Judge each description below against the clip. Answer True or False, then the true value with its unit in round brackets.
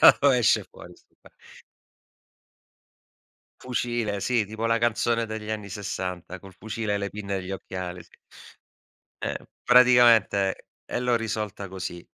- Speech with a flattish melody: False (3.3 semitones)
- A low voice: True (105 Hz)